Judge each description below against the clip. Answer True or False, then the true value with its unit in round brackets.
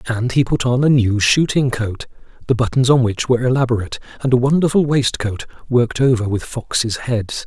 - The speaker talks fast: False (185 wpm)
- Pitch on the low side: True (125 Hz)